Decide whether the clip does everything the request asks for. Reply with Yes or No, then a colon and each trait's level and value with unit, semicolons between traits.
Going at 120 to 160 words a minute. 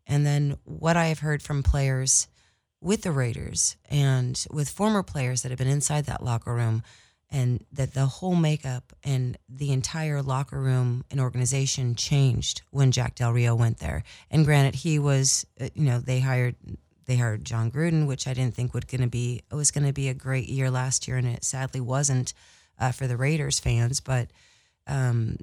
No: average, 190 wpm